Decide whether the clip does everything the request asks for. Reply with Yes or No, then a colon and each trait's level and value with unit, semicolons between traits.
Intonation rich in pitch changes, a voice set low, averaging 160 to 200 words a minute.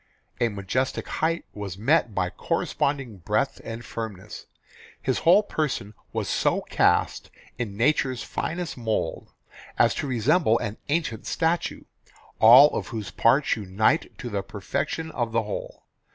No: wide, 5.9 semitones; low, 120 Hz; average, 140 wpm